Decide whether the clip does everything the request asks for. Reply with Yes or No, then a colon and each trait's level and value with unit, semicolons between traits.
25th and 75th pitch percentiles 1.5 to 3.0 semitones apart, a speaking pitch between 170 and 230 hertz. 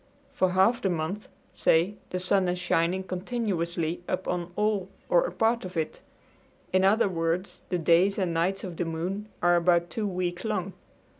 Yes: narrow, 2.5 semitones; medium, 185 Hz